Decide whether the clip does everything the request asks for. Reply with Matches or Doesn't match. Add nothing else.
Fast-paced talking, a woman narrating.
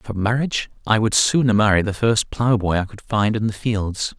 Doesn't match